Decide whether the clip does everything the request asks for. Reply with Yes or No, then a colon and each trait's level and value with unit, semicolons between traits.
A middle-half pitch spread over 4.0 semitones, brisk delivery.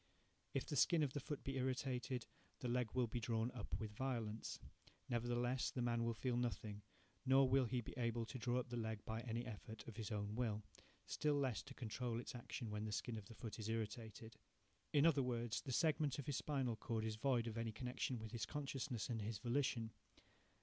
No: average, 2.7 semitones; fast, 210 wpm